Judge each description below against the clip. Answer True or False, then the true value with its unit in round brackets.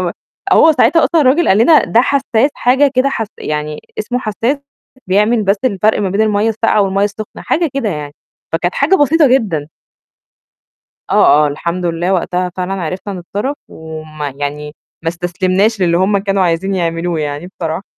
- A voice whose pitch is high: True (195 Hz)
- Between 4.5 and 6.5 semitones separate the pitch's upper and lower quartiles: True (5.4 semitones)